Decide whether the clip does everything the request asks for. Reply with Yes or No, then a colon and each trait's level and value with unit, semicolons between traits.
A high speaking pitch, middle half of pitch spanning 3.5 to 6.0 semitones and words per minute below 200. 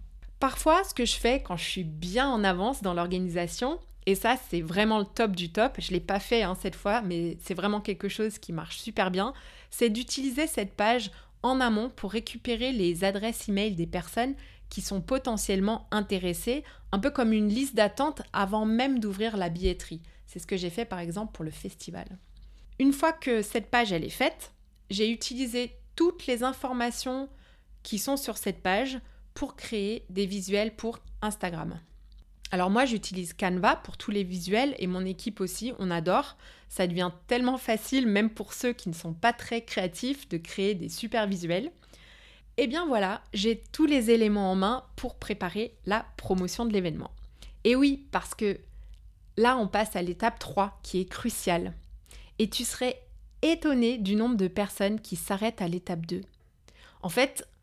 Yes: high, 210 Hz; average, 4.7 semitones; average, 180 wpm